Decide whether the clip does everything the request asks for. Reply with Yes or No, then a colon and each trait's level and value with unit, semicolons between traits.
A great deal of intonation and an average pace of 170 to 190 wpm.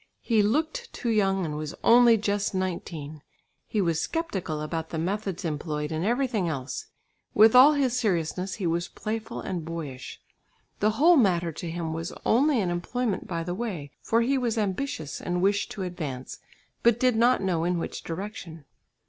Yes: wide, 5.7 semitones; average, 175 wpm